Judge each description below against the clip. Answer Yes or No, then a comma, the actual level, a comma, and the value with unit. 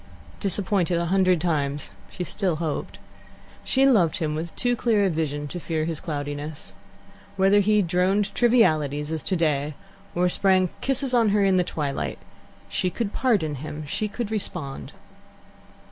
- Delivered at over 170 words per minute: No, average, 150 wpm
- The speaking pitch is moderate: Yes, medium, 180 Hz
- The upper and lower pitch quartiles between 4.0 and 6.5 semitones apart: Yes, average, 4.7 semitones